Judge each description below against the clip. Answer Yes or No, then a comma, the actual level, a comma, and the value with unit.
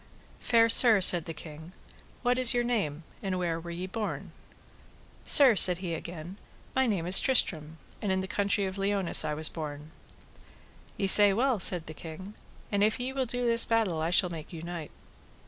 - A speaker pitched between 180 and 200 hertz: Yes, high, 190 Hz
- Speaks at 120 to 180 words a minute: No, average, 190 wpm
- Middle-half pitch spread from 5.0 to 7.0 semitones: Yes, wide, 5.4 semitones